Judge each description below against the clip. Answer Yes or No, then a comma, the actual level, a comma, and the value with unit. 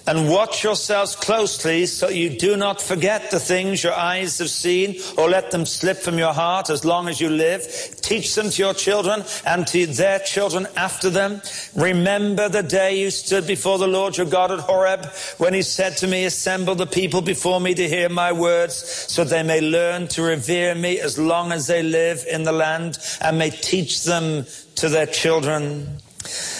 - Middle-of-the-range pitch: Yes, medium, 180 Hz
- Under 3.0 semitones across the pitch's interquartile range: Yes, narrow, 2.4 semitones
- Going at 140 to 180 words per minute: No, average, 195 wpm